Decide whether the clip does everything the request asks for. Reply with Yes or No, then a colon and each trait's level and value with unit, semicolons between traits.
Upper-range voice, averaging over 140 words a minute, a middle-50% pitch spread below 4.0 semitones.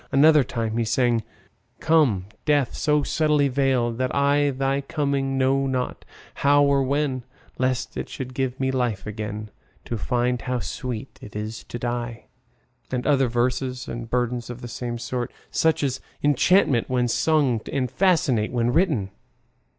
No: low, 130 Hz; average, 155 wpm; average, 2.8 semitones